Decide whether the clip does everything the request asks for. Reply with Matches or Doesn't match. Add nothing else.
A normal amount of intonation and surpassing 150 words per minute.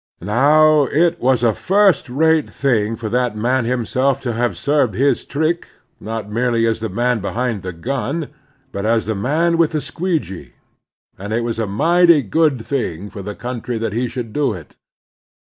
Matches